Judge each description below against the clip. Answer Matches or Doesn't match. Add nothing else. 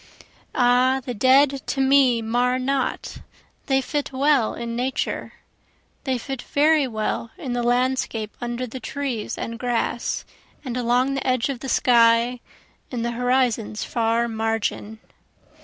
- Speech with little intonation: Matches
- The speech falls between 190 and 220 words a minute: Doesn't match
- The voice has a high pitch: Matches